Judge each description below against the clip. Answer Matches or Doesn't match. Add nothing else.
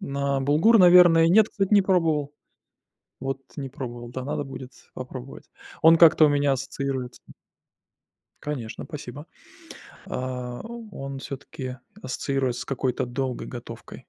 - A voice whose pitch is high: Doesn't match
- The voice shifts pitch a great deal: Doesn't match